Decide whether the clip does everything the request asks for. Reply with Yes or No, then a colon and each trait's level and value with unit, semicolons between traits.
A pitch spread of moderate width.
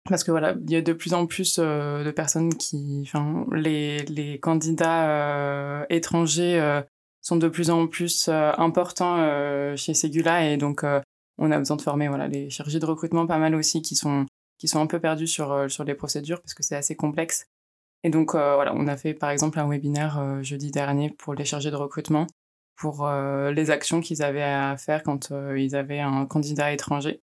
No: narrow, 2.2 semitones